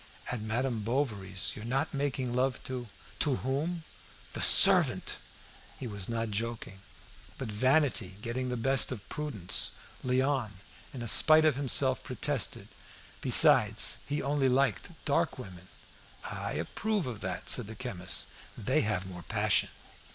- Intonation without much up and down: No, average, 4.2 semitones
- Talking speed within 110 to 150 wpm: Yes, average, 145 wpm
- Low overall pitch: Yes, low, 125 Hz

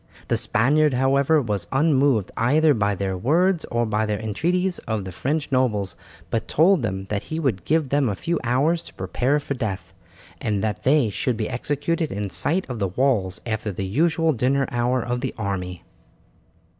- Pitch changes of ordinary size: No, wide, 6.0 semitones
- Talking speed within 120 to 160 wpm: No, average, 180 wpm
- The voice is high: No, low, 125 Hz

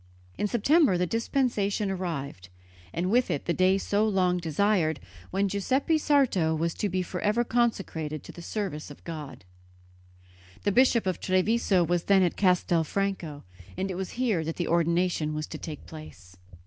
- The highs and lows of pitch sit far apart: No, average, 4.2 semitones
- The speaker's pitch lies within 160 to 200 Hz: Yes, medium, 185 Hz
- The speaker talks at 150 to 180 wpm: Yes, average, 165 wpm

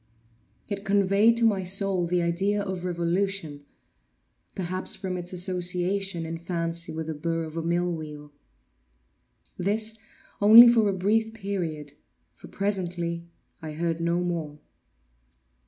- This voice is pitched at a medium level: Yes, medium, 180 Hz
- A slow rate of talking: Yes, slow, 125 wpm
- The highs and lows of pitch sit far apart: No, average, 3.0 semitones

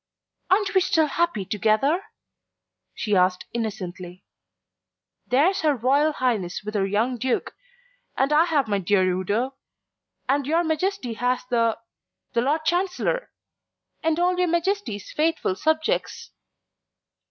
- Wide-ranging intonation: Yes, wide, 7.4 semitones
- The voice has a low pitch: No, very high, 265 Hz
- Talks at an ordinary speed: No, slow, 125 wpm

